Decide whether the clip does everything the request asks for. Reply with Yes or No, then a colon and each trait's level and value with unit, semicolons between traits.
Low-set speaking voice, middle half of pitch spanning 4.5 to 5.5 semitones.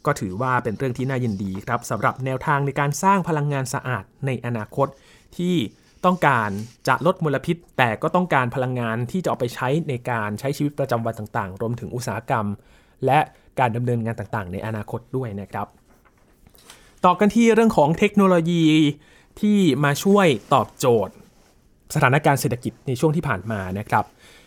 Yes: low, 130 Hz; average, 5.0 semitones